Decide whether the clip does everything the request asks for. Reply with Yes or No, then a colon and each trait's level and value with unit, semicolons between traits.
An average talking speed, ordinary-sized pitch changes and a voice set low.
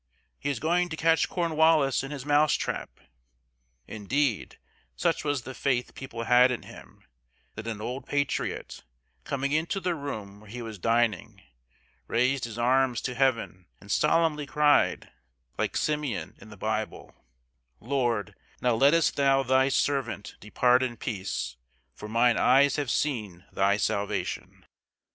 Yes: average, 145 wpm; average, 4.6 semitones; low, 130 Hz